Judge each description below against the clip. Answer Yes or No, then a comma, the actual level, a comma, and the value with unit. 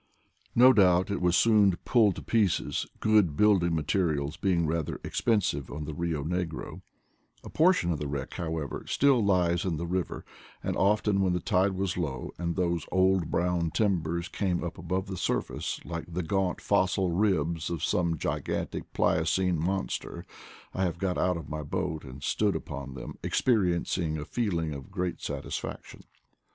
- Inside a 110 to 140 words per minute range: No, average, 170 wpm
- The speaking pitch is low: Yes, very low, 90 Hz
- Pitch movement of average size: Yes, average, 3.0 semitones